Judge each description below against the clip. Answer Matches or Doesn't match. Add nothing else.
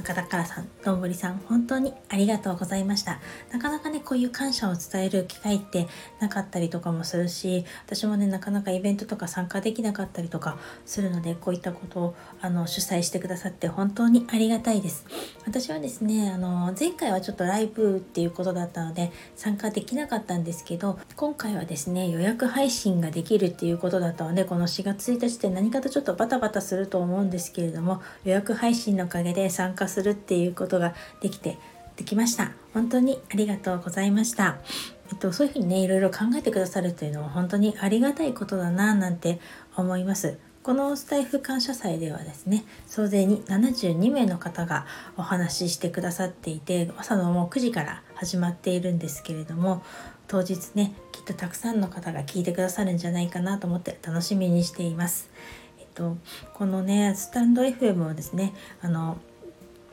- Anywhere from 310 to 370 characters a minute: Doesn't match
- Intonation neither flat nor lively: Matches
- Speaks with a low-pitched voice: Doesn't match